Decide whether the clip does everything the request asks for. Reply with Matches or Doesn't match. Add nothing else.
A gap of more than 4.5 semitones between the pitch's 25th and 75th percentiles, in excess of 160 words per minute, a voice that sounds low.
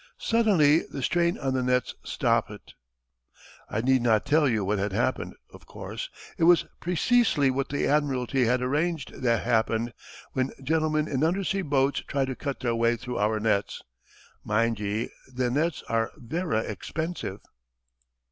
Doesn't match